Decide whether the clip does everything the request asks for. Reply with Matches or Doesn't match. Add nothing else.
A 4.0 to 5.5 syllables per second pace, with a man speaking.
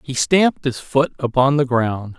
Matches